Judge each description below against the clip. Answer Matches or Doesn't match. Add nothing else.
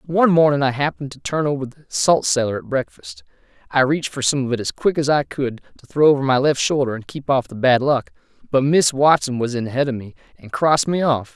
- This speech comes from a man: Matches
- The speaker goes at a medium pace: Doesn't match